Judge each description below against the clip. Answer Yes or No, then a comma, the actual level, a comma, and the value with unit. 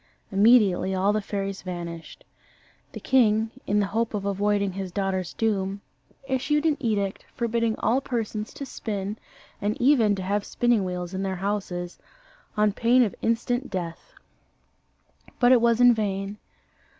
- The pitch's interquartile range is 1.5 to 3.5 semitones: Yes, average, 3.2 semitones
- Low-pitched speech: No, high, 205 Hz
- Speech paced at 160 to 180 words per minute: No, average, 150 wpm